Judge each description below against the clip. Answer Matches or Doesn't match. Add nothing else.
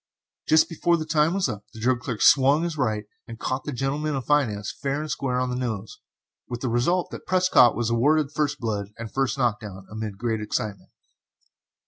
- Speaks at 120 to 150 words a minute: Doesn't match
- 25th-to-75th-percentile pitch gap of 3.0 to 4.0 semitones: Doesn't match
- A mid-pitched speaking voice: Doesn't match